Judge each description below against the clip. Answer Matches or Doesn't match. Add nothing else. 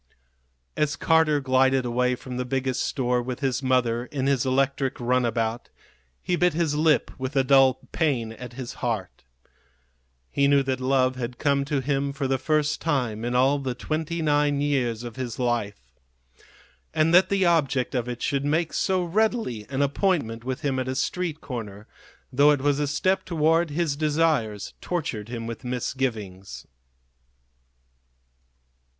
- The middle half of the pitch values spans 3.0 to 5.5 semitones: Matches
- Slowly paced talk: Doesn't match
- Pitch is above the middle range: Doesn't match